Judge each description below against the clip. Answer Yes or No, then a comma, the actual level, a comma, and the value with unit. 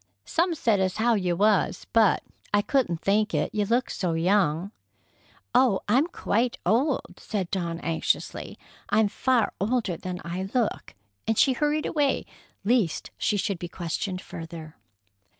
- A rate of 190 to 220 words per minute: No, average, 150 wpm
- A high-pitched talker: Yes, high, 205 Hz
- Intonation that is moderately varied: Yes, average, 5.0 semitones